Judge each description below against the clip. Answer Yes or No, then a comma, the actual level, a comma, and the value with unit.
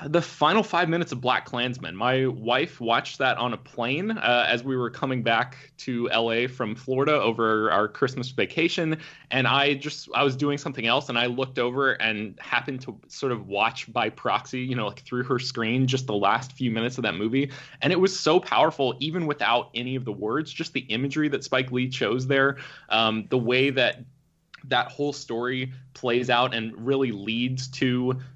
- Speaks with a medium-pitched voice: No, low, 130 Hz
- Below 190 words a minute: No, average, 200 wpm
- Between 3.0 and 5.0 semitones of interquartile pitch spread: No, narrow, 2.5 semitones